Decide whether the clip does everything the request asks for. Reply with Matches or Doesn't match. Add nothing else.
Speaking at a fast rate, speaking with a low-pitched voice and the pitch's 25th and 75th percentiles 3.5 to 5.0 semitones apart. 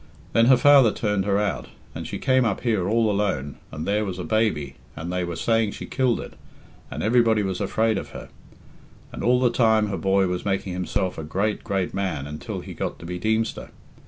Matches